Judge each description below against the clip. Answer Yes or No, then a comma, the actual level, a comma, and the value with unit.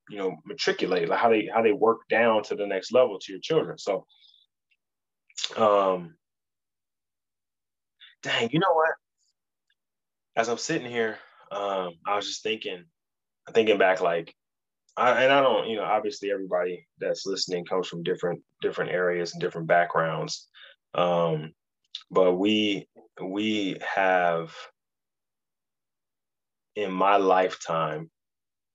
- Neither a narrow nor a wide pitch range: Yes, average, 3.1 semitones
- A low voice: Yes, very low, 95 Hz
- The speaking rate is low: Yes, slow, 125 wpm